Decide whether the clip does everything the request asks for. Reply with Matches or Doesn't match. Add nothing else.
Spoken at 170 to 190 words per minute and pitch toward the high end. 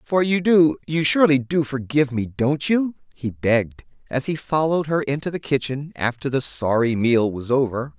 Doesn't match